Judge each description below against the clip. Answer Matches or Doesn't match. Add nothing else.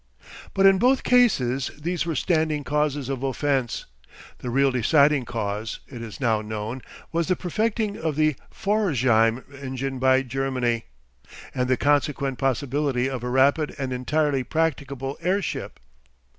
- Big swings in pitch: Doesn't match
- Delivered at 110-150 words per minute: Matches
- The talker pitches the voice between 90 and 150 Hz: Matches